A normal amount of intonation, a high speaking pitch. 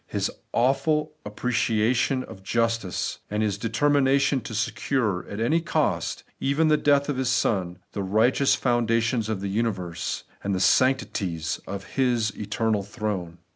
No: average, 4.5 semitones; low, 115 Hz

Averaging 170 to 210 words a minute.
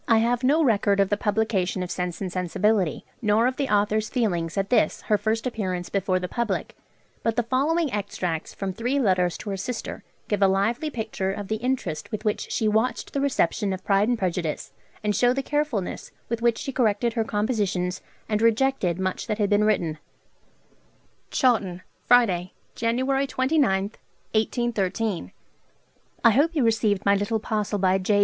Yes: average, 175 wpm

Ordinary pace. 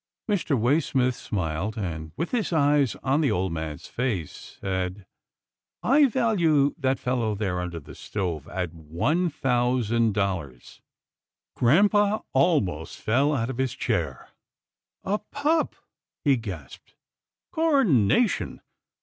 No: slow, 130 wpm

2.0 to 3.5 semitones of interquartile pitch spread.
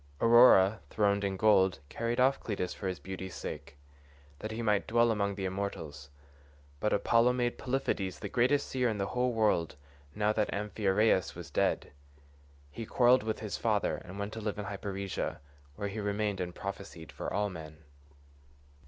Yes: average, 2.9 semitones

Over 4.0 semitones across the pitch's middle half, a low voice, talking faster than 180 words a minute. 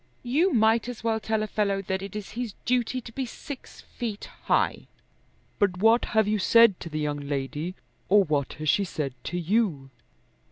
No: average, 4.9 semitones; high, 205 Hz; average, 190 wpm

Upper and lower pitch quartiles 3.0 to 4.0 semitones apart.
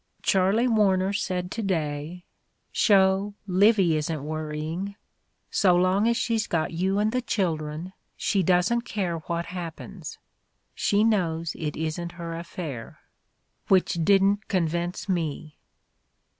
Yes: average, 3.5 semitones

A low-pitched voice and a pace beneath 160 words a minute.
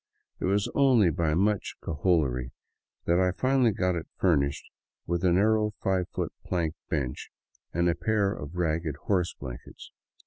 Yes: very low, 90 Hz; average, 150 wpm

